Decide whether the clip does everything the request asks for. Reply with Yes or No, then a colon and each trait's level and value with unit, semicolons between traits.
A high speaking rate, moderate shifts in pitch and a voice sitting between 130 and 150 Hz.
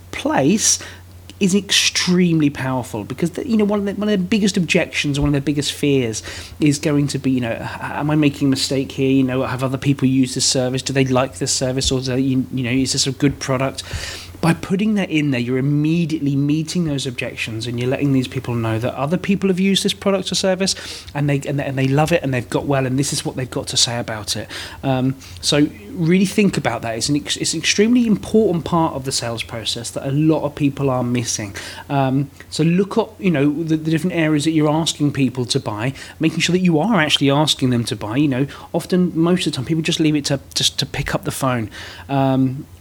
Yes: fast, 240 wpm; average, 3.9 semitones; medium, 140 Hz